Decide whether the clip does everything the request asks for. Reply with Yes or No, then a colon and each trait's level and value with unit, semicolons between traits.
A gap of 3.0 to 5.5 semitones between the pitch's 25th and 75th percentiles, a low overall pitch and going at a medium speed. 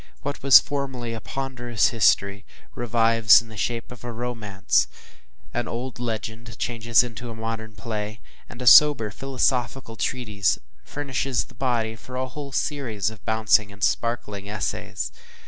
No: narrow, 2.4 semitones; low, 115 Hz; average, 145 wpm